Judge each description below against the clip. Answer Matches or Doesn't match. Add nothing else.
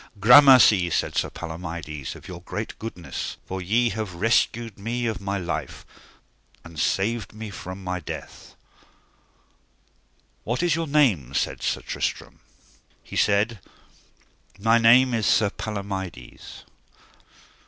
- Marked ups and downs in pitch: Doesn't match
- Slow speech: Matches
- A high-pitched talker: Doesn't match